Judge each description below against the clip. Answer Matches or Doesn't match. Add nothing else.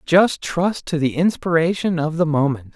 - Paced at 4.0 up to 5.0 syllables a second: Matches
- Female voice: Doesn't match